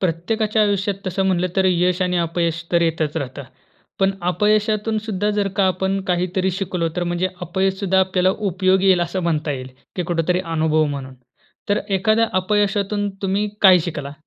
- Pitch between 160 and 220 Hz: Yes, medium, 185 Hz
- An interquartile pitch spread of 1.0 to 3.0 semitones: Yes, narrow, 2.5 semitones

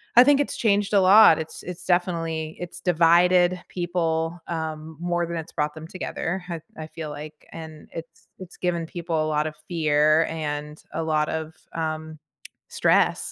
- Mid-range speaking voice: Yes, medium, 165 Hz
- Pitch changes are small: Yes, narrow, 2.1 semitones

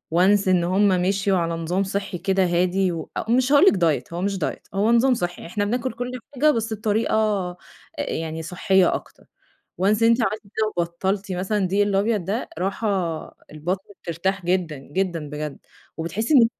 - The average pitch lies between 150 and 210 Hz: Yes, high, 190 Hz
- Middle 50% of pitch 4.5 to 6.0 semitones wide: No, average, 3.5 semitones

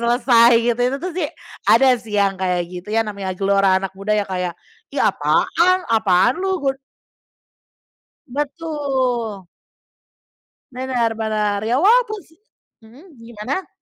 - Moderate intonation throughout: No, wide, 6.0 semitones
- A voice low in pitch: No, high, 235 Hz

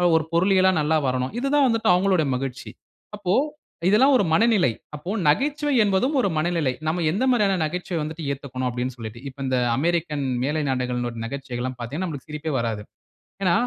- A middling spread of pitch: No, wide, 6.6 semitones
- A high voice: No, medium, 155 Hz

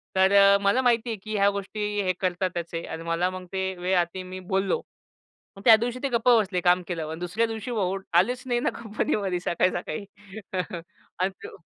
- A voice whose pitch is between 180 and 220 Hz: Yes, high, 190 Hz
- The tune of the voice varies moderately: Yes, average, 3.2 semitones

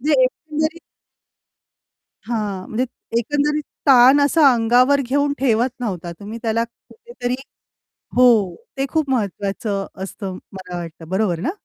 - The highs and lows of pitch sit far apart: Yes, wide, 5.8 semitones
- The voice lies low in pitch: No, high, 240 Hz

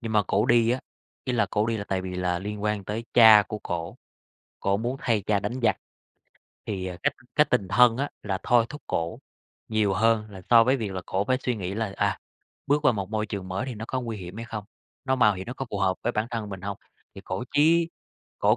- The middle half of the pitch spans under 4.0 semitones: Yes, average, 3.4 semitones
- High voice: No, low, 105 Hz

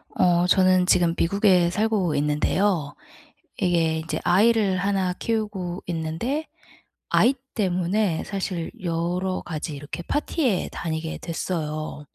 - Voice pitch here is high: No, medium, 180 Hz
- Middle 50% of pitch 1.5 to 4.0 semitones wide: Yes, average, 3.2 semitones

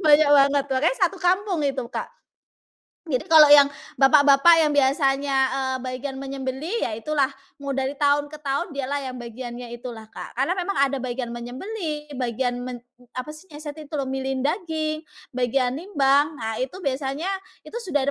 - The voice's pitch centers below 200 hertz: No, very high, 275 Hz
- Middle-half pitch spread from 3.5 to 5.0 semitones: No, average, 2.8 semitones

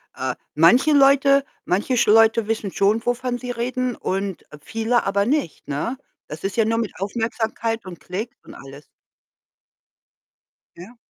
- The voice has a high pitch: Yes, high, 225 Hz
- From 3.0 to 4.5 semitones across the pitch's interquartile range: Yes, average, 3.9 semitones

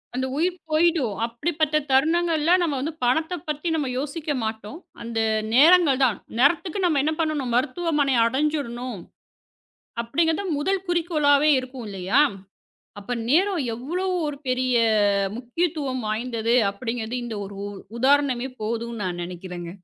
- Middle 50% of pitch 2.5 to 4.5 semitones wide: No, average, 5.2 semitones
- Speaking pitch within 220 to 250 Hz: No, very high, 275 Hz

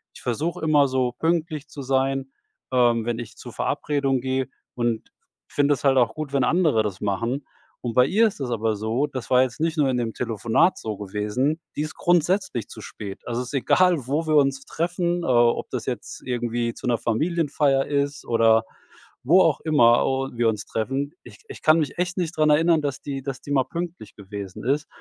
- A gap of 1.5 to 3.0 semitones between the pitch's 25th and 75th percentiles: No, average, 4.5 semitones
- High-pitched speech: No, low, 135 Hz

